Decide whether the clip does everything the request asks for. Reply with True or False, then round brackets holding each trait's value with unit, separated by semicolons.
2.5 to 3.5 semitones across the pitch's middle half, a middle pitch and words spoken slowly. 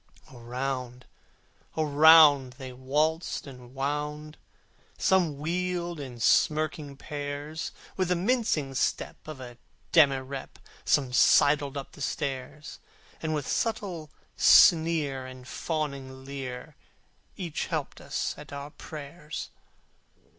True (3.0 semitones; 145 Hz; 105 wpm)